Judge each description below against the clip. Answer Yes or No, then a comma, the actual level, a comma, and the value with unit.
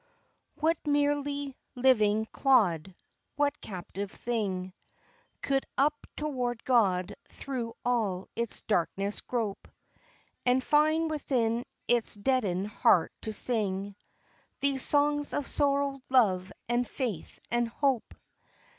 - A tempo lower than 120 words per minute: Yes, slow, 105 wpm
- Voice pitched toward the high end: Yes, high, 240 Hz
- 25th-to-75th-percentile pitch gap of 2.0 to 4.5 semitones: No, average, 5.3 semitones